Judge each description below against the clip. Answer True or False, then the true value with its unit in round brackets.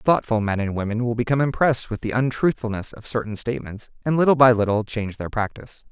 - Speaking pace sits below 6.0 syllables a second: False (6.4 syllables/s)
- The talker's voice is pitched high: False (120 Hz)